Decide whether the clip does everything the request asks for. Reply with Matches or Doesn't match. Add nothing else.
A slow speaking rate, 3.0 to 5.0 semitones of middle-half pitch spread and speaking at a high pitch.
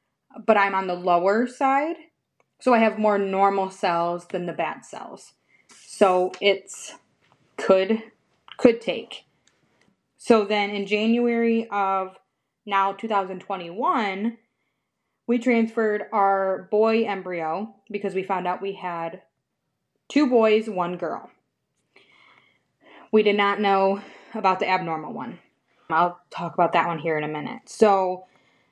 Matches